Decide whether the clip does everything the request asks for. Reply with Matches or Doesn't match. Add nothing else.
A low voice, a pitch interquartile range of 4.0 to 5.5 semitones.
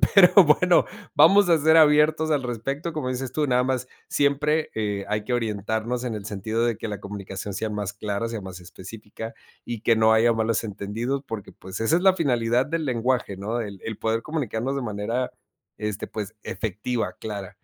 Matches